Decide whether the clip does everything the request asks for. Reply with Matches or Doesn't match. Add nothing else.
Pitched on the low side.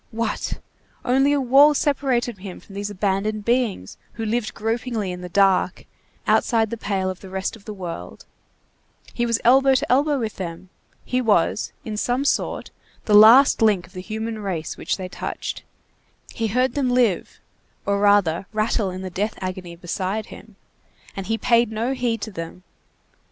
Doesn't match